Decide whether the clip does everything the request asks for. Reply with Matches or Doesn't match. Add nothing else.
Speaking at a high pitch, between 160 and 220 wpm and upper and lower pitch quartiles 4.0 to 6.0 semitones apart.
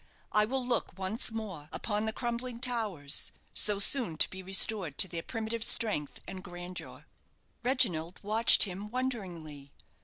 Doesn't match